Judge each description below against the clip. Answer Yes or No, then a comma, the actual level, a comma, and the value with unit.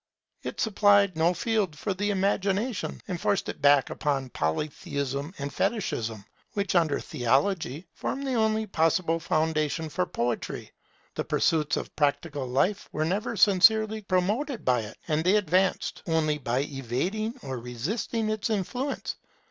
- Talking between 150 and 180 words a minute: No, average, 140 wpm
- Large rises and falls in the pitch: Yes, wide, 6.3 semitones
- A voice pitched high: No, medium, 170 Hz